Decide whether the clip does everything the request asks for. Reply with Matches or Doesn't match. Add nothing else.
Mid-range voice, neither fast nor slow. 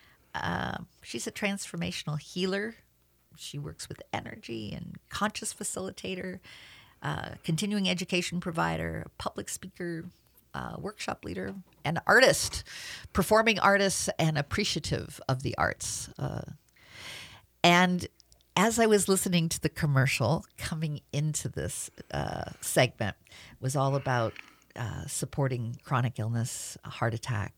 Doesn't match